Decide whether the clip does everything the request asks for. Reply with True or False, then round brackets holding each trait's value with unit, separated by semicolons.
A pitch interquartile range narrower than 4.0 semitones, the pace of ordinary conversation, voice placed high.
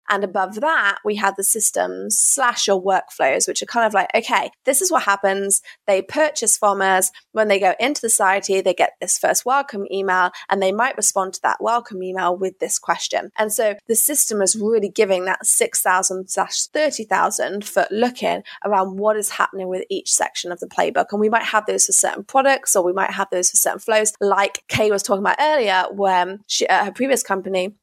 False (2.8 semitones; 215 wpm; 200 Hz)